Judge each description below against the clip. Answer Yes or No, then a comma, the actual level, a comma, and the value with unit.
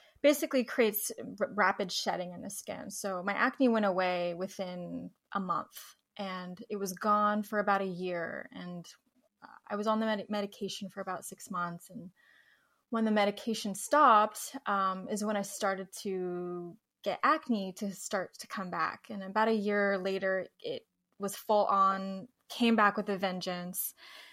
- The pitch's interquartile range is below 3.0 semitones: Yes, narrow, 2.4 semitones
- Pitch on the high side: Yes, high, 205 Hz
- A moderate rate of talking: Yes, average, 165 wpm